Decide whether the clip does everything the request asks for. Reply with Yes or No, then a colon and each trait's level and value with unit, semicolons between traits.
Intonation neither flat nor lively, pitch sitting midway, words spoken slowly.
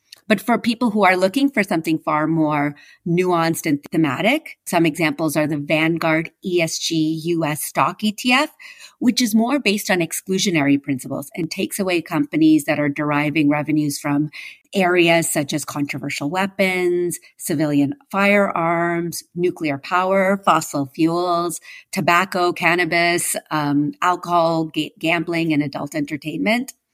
Yes: average, 3.9 semitones; medium, 170 Hz; slow, 130 wpm